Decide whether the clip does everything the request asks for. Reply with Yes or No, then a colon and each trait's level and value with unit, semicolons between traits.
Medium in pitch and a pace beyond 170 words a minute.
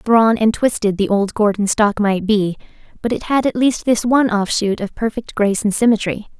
No: high, 215 Hz; fast, 205 wpm